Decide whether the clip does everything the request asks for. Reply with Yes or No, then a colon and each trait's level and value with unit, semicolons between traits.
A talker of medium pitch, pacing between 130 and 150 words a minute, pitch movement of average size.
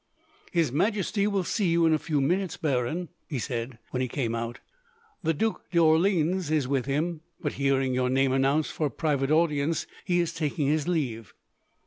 No: medium, 150 Hz; average, 180 wpm; average, 4.0 semitones